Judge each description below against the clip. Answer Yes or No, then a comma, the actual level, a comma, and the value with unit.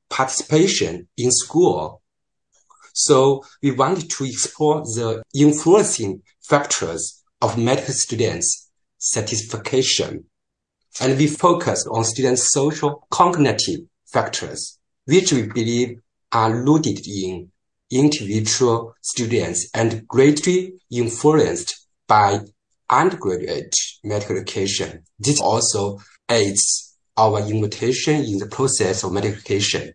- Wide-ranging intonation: No, average, 5.0 semitones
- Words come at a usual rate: No, slow, 100 wpm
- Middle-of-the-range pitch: No, low, 120 Hz